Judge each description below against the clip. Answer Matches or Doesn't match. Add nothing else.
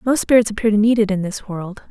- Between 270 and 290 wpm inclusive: Matches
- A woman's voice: Matches